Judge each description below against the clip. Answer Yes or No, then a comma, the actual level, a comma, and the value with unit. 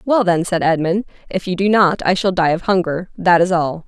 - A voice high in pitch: No, medium, 180 Hz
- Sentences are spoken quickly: Yes, fast, 230 wpm